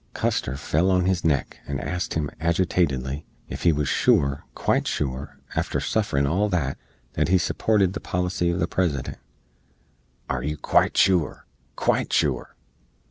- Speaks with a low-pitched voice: Yes, very low, 85 Hz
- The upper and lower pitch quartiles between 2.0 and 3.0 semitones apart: No, average, 4.5 semitones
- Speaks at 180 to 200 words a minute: No, average, 150 wpm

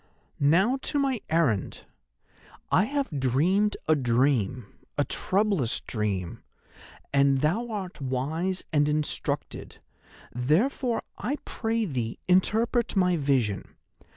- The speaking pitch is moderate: Yes, medium, 155 Hz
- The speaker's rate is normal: No, slow, 105 wpm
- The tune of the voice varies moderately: No, wide, 8.1 semitones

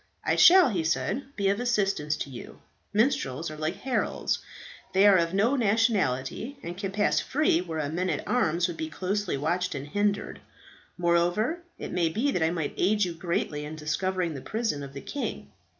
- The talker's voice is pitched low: No, medium, 180 Hz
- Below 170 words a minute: No, average, 190 wpm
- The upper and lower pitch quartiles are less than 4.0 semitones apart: No, average, 4.9 semitones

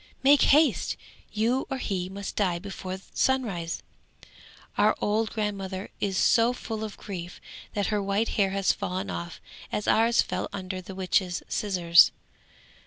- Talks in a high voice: Yes, high, 200 Hz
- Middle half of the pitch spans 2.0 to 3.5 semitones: Yes, average, 2.9 semitones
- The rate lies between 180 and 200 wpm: No, average, 145 wpm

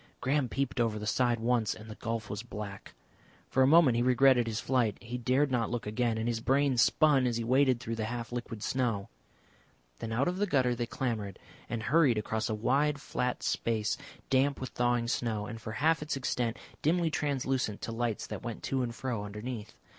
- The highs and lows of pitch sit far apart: No, average, 2.8 semitones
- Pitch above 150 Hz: No, low, 120 Hz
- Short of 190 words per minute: No, fast, 205 wpm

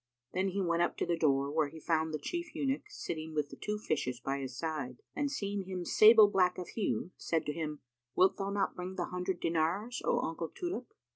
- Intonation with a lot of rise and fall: No, average, 4.2 semitones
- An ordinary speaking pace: No, fast, 220 wpm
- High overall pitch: No, medium, 175 Hz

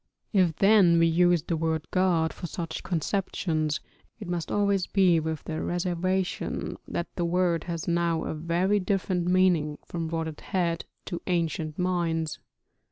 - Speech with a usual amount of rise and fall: No, narrow, 2.0 semitones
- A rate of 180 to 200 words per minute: No, average, 155 wpm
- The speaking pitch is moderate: Yes, medium, 170 Hz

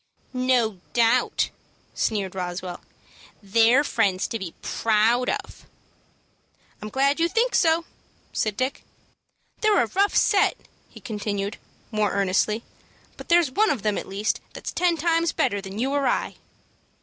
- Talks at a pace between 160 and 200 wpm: No, average, 140 wpm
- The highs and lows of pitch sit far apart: Yes, wide, 6.3 semitones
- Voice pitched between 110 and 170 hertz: No, high, 230 Hz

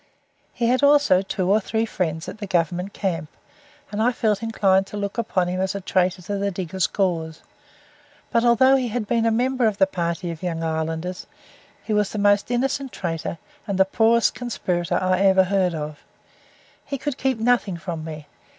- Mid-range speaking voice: No, high, 195 Hz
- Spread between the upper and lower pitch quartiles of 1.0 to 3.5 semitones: No, average, 4.3 semitones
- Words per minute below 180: No, average, 190 wpm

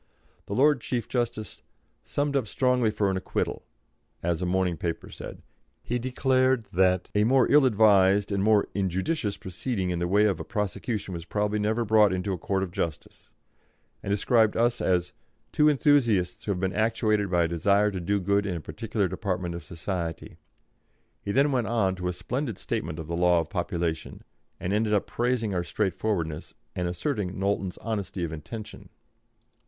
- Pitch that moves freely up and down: No, average, 4.0 semitones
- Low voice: Yes, low, 100 Hz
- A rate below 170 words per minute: No, average, 180 wpm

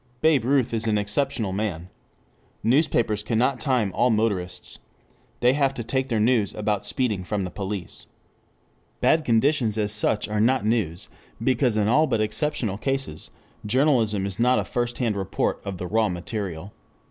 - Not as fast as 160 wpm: No, average, 165 wpm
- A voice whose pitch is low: Yes, low, 110 Hz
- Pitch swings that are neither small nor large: Yes, average, 3.8 semitones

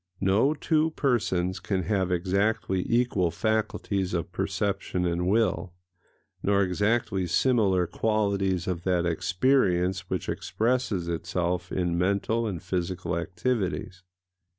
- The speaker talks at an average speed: No, slow, 110 wpm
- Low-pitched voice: Yes, very low, 95 Hz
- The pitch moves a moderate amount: Yes, average, 3.3 semitones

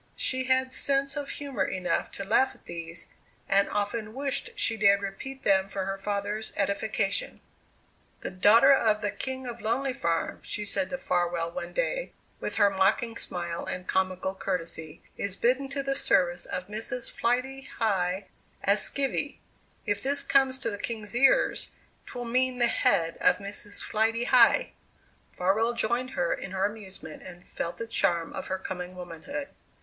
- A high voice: Yes, high, 210 Hz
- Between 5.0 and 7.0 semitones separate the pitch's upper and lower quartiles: Yes, average, 5.3 semitones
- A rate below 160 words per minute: No, average, 165 wpm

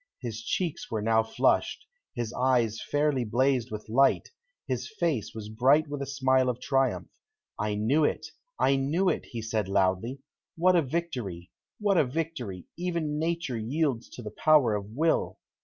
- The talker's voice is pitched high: No, low, 130 Hz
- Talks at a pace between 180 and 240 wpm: No, average, 165 wpm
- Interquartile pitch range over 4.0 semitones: Yes, wide, 5.5 semitones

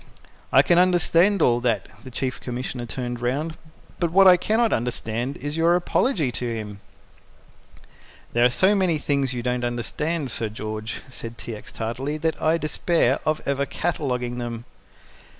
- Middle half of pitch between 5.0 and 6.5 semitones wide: Yes, wide, 5.4 semitones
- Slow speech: No, average, 160 wpm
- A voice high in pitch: No, low, 130 Hz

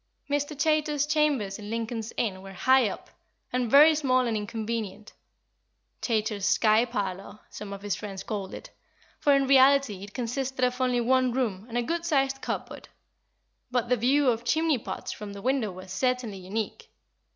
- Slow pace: No, average, 170 wpm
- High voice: Yes, high, 240 Hz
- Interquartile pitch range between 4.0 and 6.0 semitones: Yes, average, 4.4 semitones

